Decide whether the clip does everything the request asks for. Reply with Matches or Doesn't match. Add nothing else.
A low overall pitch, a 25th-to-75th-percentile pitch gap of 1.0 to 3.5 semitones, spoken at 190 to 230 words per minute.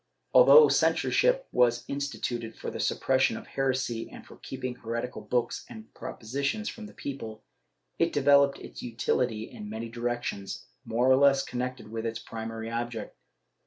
Doesn't match